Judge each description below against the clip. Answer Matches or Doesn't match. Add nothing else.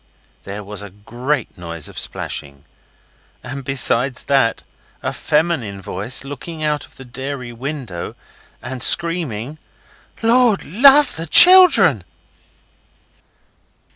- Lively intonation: Matches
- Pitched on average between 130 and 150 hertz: Matches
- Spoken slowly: Matches